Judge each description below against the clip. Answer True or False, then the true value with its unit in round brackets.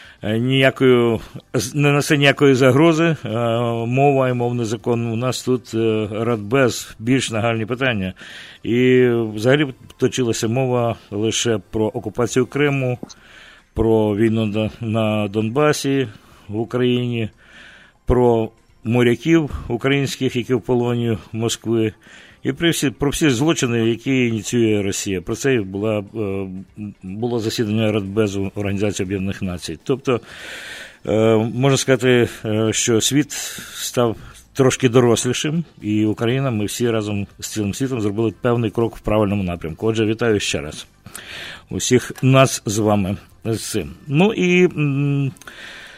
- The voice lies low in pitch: True (115 Hz)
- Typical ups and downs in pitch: True (3.2 semitones)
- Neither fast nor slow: False (115 wpm)